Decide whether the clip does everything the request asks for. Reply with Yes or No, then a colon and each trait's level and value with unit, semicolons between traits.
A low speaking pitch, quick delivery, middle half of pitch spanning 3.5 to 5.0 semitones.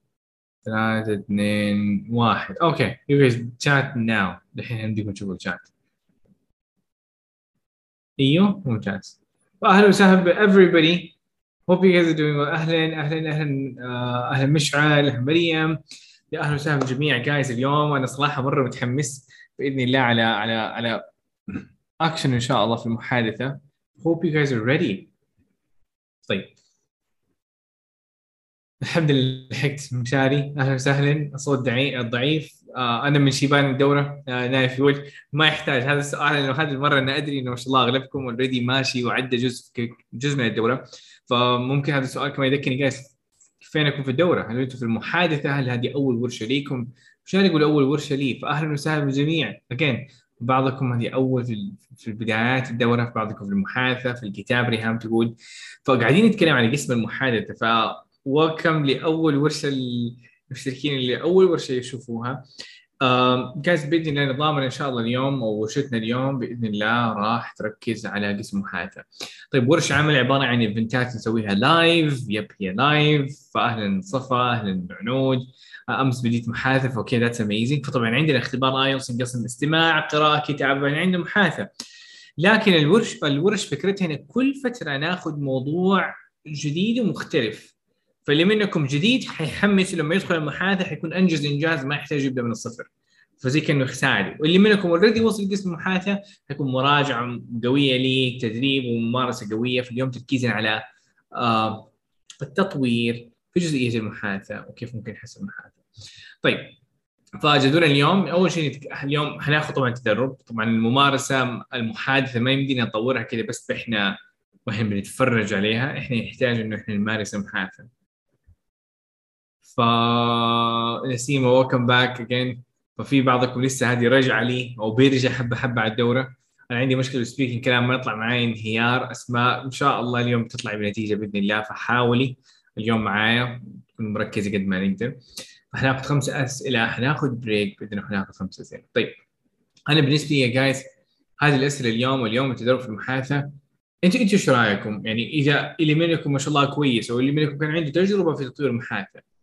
Yes: low, 130 Hz; fast, 140 wpm; average, 3.8 semitones